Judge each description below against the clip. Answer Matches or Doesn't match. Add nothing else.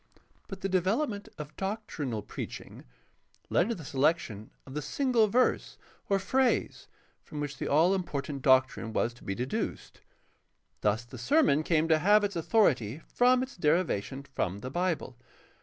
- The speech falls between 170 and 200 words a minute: Doesn't match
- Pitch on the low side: Doesn't match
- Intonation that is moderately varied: Doesn't match